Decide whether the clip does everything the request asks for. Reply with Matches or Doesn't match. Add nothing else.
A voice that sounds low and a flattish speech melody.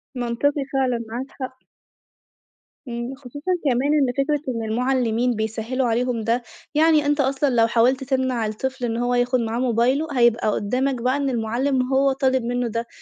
Doesn't match